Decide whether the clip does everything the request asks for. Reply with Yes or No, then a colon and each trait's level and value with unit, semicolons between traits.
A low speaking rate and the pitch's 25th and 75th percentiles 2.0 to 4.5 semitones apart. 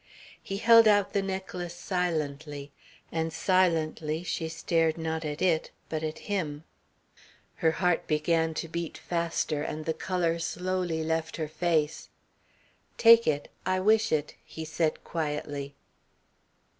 Yes: slow, 130 wpm; narrow, 2.5 semitones